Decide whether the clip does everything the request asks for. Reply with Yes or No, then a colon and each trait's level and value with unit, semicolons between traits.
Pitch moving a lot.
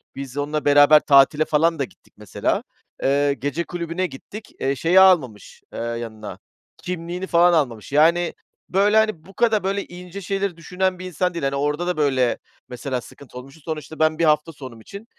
No: average, 4.5 semitones